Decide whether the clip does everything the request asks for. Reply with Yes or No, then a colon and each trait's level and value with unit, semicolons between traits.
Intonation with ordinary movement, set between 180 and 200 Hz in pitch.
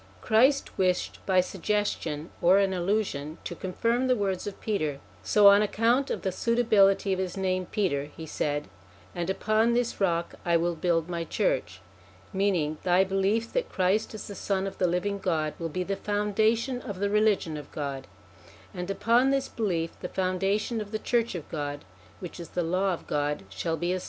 Yes: average, 3.8 semitones; high, 190 Hz